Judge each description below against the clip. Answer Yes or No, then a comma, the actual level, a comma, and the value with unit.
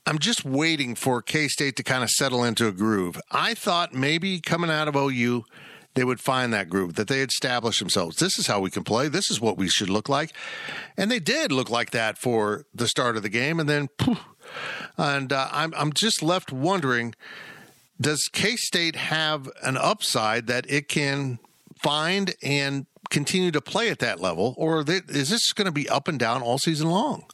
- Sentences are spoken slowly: No, fast, 205 wpm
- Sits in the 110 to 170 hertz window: Yes, medium, 140 Hz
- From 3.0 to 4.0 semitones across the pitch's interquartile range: No, average, 5.1 semitones